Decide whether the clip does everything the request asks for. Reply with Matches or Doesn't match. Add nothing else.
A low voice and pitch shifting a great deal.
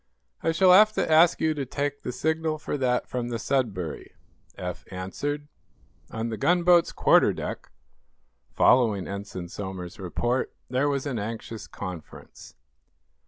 Matches